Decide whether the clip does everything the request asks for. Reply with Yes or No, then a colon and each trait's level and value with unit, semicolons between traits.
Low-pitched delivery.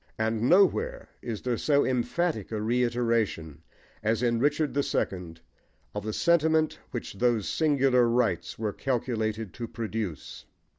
Yes: low, 120 Hz